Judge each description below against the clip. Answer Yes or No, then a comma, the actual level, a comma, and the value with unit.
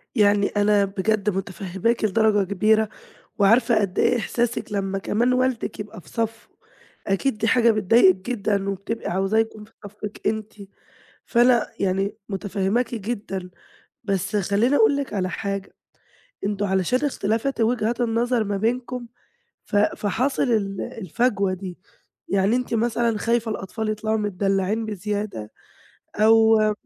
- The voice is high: Yes, high, 215 Hz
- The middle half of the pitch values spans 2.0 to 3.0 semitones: Yes, average, 2.7 semitones